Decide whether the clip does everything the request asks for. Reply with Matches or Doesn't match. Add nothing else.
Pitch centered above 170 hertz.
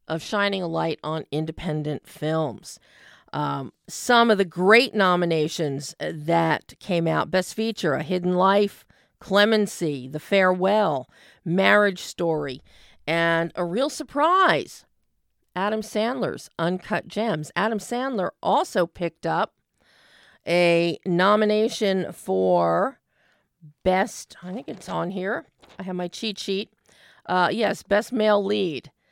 Matches